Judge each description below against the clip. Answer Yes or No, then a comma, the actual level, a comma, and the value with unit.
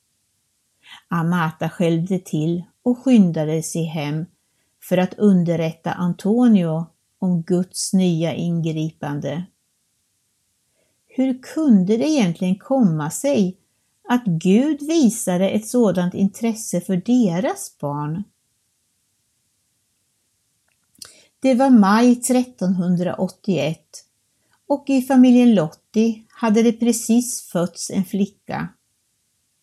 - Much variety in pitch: Yes, wide, 5.9 semitones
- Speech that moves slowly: Yes, slow, 90 wpm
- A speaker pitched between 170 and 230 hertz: Yes, medium, 185 Hz